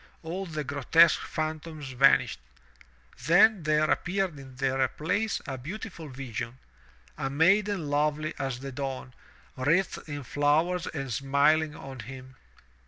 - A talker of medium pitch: Yes, medium, 145 Hz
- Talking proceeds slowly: Yes, slow, 130 wpm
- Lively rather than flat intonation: No, average, 3.6 semitones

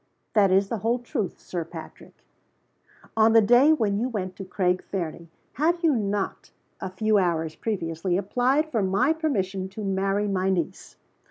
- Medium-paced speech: Yes, average, 165 wpm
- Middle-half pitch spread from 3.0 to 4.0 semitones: Yes, average, 3.6 semitones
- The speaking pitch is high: Yes, high, 200 Hz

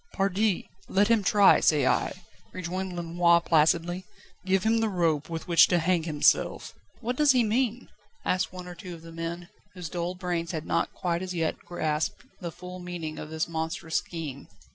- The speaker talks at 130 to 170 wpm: No, average, 185 wpm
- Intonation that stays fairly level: Yes, narrow, 2.2 semitones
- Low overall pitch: No, medium, 175 Hz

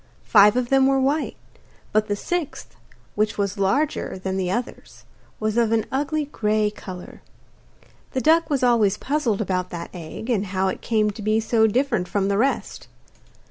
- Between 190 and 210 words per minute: No, average, 175 wpm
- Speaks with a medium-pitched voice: No, high, 215 Hz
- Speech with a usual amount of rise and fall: Yes, average, 5.0 semitones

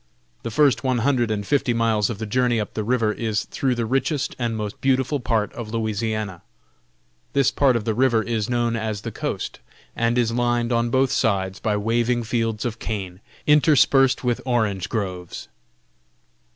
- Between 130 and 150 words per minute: No, average, 175 wpm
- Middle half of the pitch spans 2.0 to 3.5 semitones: Yes, narrow, 2.5 semitones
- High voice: No, low, 115 Hz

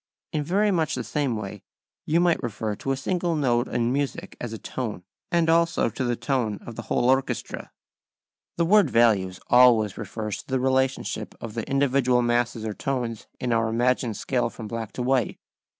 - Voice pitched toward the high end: No, low, 125 Hz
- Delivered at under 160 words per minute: No, average, 185 wpm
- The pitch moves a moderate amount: Yes, average, 3.4 semitones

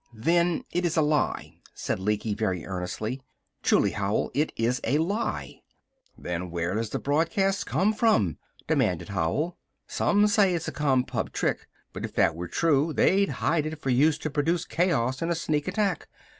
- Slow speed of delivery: No, average, 170 wpm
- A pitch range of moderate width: No, wide, 8.3 semitones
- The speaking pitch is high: No, medium, 150 Hz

